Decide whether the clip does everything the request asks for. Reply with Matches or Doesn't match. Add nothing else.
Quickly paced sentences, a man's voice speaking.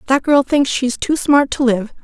Doesn't match